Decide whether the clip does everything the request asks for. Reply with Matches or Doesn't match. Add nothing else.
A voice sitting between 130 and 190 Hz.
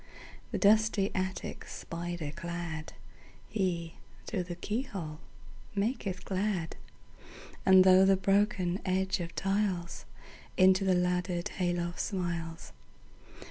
Matches